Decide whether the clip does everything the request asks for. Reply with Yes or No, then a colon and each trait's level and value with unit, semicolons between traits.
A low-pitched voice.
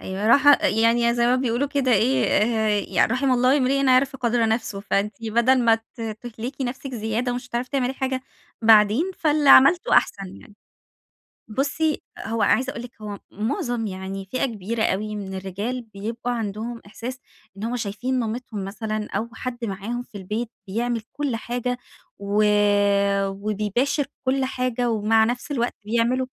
No: high, 235 Hz